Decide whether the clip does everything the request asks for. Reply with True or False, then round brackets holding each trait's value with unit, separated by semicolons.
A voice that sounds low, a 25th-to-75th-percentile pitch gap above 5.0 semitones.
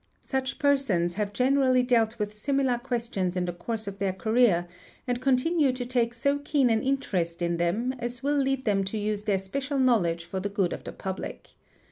False (230 Hz; 5.4 semitones)